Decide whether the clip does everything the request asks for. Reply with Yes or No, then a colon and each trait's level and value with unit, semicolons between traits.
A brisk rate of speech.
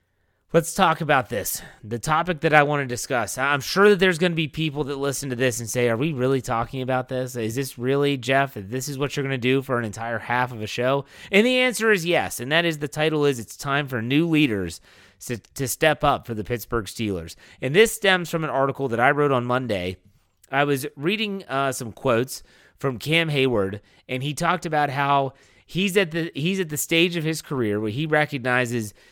Yes: fast, 225 wpm